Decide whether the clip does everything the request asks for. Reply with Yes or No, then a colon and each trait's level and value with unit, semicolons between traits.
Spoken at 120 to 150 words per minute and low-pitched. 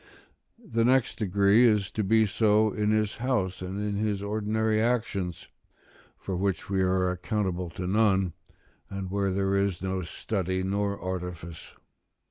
Yes: average, 145 wpm; low, 100 Hz